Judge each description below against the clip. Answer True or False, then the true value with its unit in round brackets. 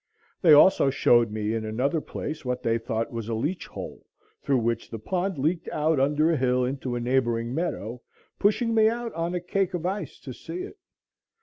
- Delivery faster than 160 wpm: True (200 wpm)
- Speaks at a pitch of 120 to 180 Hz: True (140 Hz)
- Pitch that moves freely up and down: True (6.9 semitones)